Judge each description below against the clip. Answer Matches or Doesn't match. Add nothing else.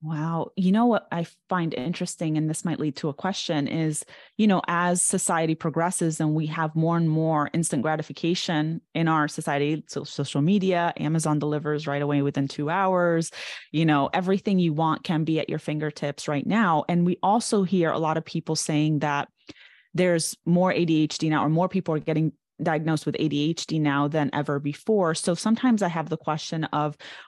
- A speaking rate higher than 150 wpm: Matches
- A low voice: Doesn't match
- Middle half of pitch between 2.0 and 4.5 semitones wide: Matches